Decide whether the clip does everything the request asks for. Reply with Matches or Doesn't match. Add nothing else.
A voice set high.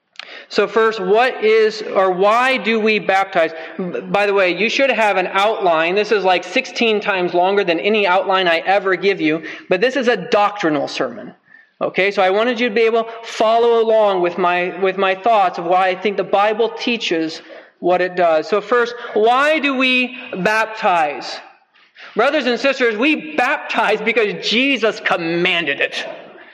Matches